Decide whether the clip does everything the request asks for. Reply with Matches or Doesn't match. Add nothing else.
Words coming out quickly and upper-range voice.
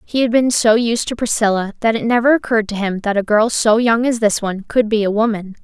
Matches